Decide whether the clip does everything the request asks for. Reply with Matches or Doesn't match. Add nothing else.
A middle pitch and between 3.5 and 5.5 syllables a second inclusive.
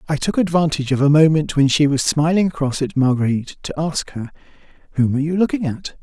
Doesn't match